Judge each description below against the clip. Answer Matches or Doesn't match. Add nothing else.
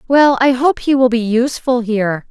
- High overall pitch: Matches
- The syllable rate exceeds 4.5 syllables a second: Matches